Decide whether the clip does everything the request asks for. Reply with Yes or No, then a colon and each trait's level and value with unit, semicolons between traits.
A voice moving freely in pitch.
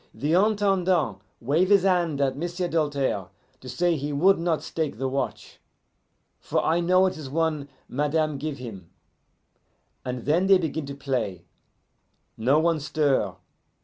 No: average, 4.3 semitones